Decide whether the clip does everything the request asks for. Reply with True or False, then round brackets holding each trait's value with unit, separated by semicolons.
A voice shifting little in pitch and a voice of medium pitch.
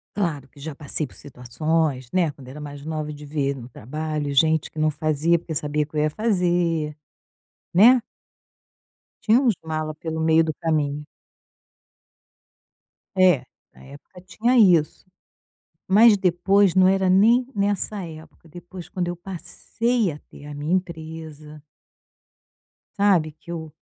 False (3.8 semitones; 160 Hz)